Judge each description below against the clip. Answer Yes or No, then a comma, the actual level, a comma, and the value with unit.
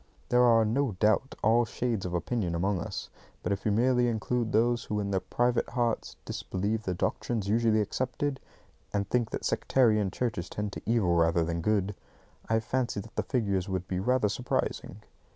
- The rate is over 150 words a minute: Yes, average, 180 wpm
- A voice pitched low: Yes, low, 110 Hz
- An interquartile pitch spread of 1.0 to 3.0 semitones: No, average, 3.7 semitones